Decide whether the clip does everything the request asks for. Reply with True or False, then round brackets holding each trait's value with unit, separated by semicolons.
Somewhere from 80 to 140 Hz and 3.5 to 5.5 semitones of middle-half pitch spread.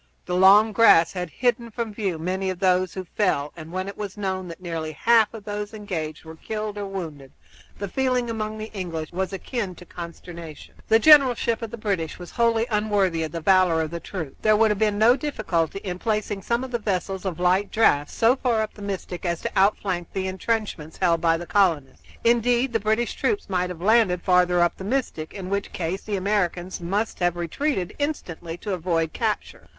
False (190 Hz; 3.9 semitones)